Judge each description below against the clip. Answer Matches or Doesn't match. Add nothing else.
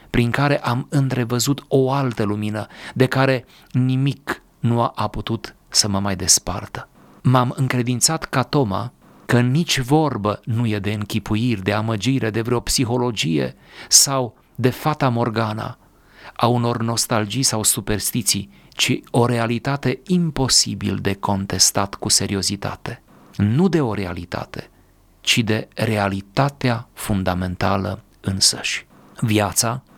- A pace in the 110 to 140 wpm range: Matches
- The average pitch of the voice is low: Matches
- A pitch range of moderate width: Matches